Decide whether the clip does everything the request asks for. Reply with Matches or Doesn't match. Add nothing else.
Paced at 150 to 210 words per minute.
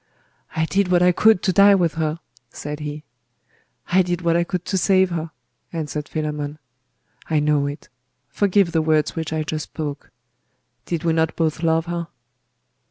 Matches